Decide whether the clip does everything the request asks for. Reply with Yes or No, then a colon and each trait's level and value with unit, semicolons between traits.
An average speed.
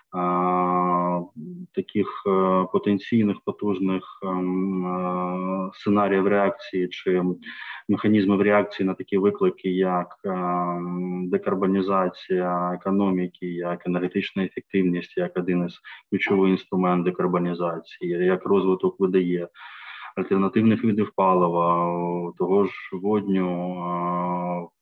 No: slow, 75 wpm